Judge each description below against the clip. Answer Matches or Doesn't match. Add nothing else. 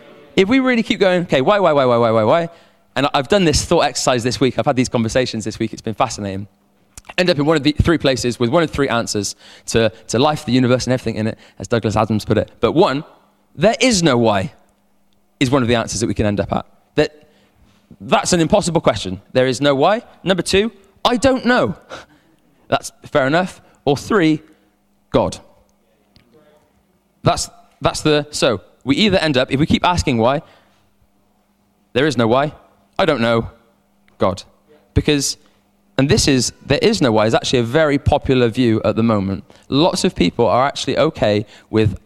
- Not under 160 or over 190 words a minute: Doesn't match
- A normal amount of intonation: Doesn't match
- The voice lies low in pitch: Matches